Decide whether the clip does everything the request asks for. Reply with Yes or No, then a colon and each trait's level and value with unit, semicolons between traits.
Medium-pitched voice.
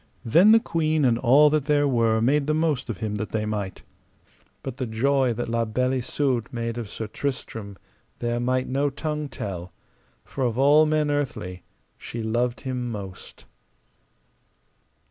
No: low, 125 Hz